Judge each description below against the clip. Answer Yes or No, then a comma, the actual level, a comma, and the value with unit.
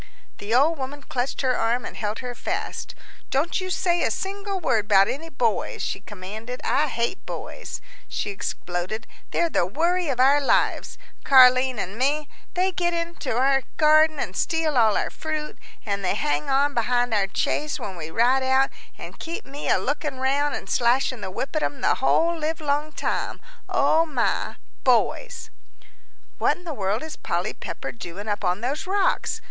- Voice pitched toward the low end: No, very high, 270 Hz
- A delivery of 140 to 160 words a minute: No, average, 175 wpm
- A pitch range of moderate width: No, wide, 5.7 semitones